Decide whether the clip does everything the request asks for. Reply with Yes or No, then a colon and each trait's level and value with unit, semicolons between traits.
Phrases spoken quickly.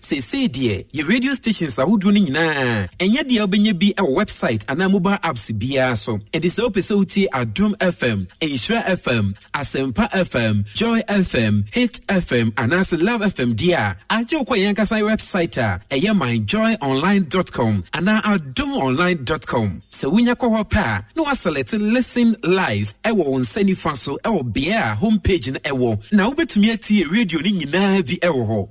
No: average, 185 wpm